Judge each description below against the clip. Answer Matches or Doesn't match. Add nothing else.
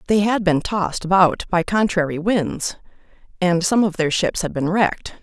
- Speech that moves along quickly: Doesn't match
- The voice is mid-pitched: Matches